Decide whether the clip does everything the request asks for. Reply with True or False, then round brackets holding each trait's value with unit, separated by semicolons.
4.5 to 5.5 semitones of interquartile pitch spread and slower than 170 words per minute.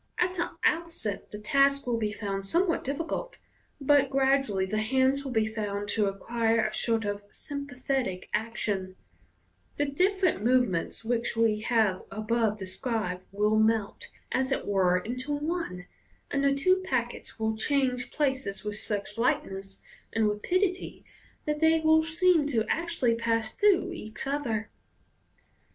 True (5.2 semitones; 145 wpm)